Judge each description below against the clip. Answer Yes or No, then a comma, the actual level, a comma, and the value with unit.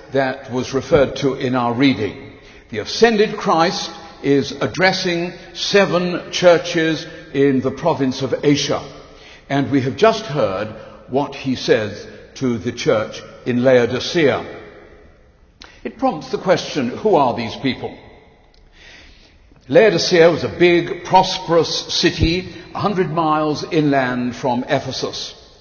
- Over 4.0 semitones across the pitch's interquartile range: Yes, average, 5.2 semitones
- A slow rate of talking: Yes, slow, 120 wpm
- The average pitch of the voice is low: No, medium, 145 Hz